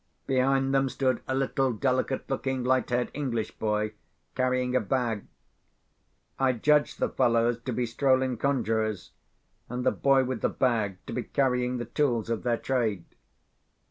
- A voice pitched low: Yes, low, 125 Hz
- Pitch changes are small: Yes, narrow, 2.3 semitones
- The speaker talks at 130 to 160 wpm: Yes, average, 155 wpm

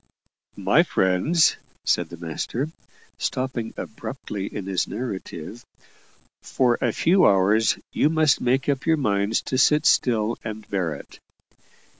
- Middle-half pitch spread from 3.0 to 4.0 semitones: No, average, 5.1 semitones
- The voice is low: Yes, low, 115 Hz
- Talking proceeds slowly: Yes, slow, 130 wpm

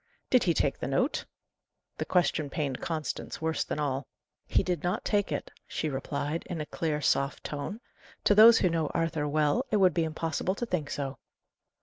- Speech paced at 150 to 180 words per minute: No, average, 190 wpm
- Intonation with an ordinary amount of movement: Yes, average, 3.7 semitones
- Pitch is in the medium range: Yes, medium, 160 Hz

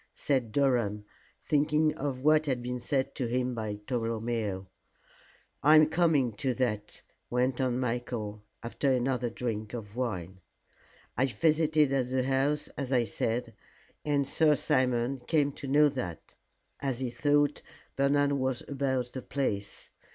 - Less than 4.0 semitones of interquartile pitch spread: Yes, average, 3.1 semitones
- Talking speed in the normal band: Yes, average, 145 wpm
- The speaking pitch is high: No, low, 130 Hz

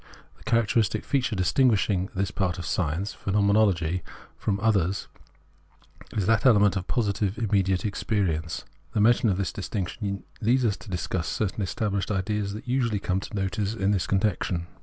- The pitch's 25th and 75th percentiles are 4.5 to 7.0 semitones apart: No, narrow, 2.5 semitones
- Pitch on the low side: Yes, low, 100 Hz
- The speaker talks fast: No, average, 165 wpm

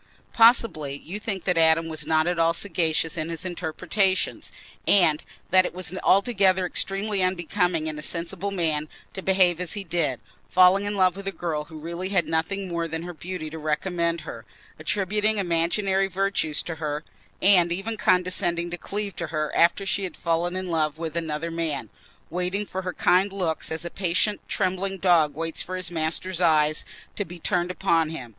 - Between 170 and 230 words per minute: Yes, average, 180 wpm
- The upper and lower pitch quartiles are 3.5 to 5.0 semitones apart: No, average, 2.8 semitones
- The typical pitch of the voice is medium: Yes, medium, 175 Hz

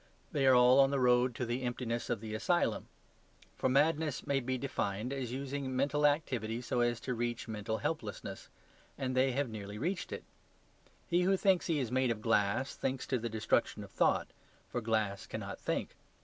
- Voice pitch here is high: No, low, 125 Hz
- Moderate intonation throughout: Yes, average, 3.4 semitones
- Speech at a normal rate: Yes, average, 190 wpm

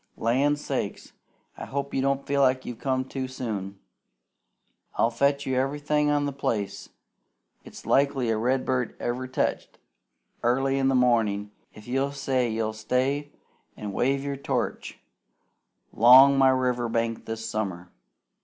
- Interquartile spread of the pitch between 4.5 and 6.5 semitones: No, average, 3.2 semitones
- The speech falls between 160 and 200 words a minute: No, average, 140 wpm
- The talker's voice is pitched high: No, low, 130 Hz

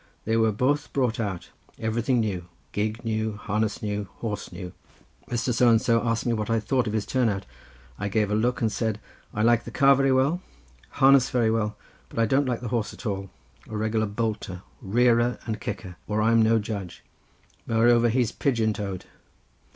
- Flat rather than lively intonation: Yes, narrow, 2.1 semitones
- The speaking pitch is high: No, low, 110 Hz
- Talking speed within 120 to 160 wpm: No, average, 190 wpm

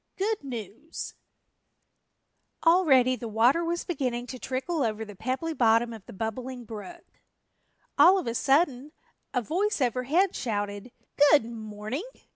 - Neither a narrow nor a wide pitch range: No, wide, 6.3 semitones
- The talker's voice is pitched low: No, very high, 255 Hz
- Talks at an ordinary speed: No, slow, 130 wpm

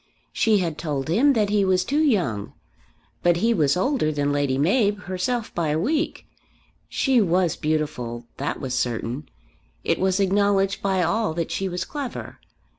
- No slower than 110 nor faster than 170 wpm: Yes, average, 165 wpm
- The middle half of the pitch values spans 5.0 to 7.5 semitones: Yes, wide, 5.5 semitones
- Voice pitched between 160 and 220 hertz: Yes, medium, 185 Hz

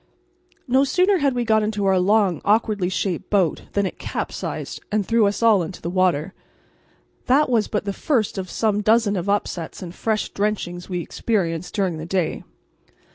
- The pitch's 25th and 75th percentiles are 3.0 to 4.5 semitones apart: Yes, average, 3.3 semitones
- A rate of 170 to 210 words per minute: Yes, average, 180 wpm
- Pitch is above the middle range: Yes, high, 205 Hz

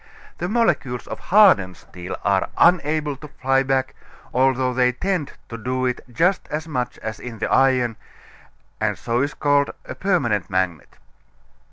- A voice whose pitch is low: Yes, low, 130 Hz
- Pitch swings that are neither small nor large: Yes, average, 4.1 semitones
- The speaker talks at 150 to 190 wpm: Yes, average, 160 wpm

